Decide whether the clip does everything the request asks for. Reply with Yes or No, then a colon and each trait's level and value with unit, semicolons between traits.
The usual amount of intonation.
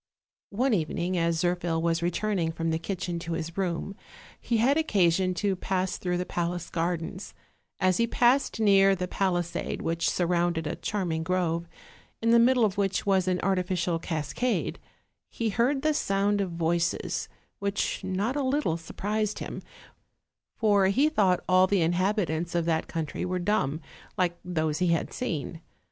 Yes: average, 3.3 semitones